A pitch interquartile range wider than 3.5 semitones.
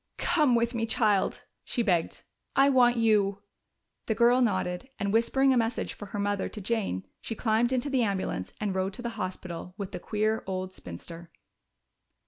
Yes: average, 4.0 semitones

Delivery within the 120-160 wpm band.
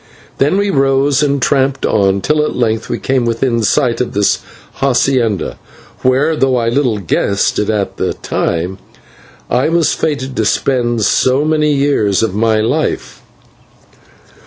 Yes: average, 150 wpm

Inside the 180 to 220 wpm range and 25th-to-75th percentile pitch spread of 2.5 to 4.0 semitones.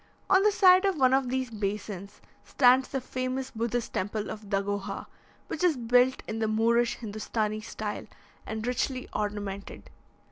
No: average, 150 wpm; average, 3.7 semitones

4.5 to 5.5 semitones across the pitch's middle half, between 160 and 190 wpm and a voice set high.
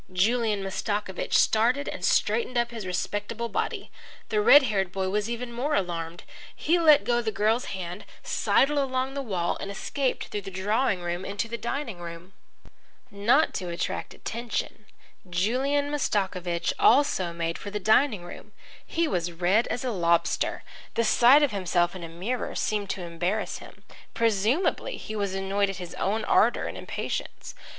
Yes: average, 4.9 semitones; average, 165 wpm; high, 210 Hz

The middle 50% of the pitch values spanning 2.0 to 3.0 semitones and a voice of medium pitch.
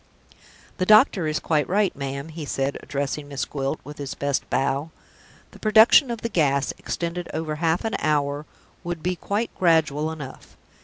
No: average, 3.9 semitones; medium, 155 Hz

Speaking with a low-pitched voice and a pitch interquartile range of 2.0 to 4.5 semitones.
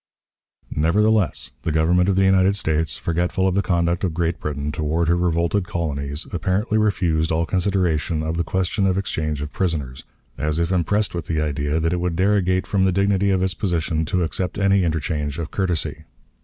Yes: very low, 85 Hz; average, 3.2 semitones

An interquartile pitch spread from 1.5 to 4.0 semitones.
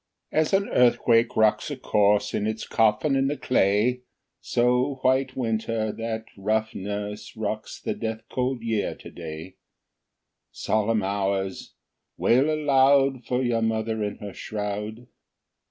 Yes: average, 3.4 semitones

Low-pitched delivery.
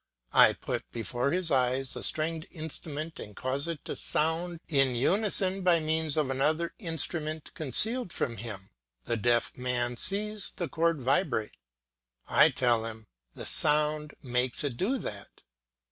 No: medium, 150 Hz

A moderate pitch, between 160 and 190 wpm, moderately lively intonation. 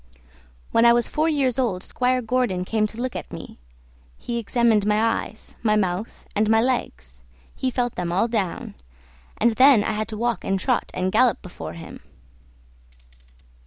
No: high, 225 Hz; average, 170 wpm; average, 3.7 semitones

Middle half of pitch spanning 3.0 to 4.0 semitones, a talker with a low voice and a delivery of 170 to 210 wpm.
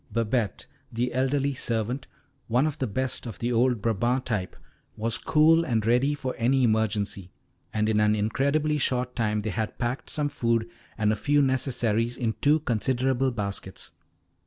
No: average, 3.3 semitones; low, 120 Hz; average, 160 wpm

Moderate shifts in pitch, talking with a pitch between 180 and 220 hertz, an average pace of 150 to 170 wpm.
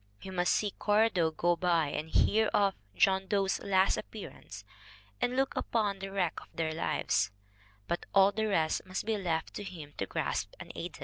No: average, 3.5 semitones; high, 190 Hz; average, 190 wpm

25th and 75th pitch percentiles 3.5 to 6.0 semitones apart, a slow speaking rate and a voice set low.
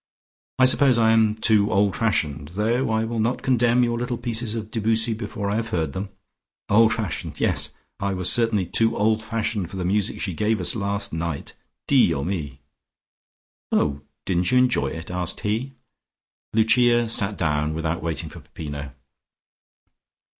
No: average, 4.5 semitones; average, 160 wpm; low, 105 Hz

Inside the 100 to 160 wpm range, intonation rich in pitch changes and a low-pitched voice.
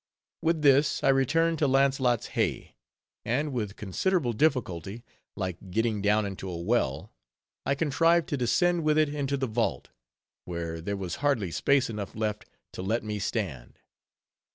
Yes: average, 155 wpm; wide, 6.2 semitones; low, 120 Hz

